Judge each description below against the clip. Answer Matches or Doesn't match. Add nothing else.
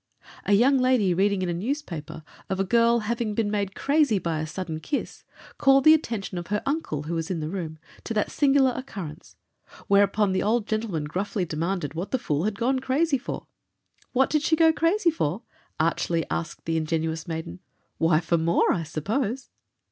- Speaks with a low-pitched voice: Doesn't match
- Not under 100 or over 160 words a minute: Doesn't match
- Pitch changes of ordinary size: Doesn't match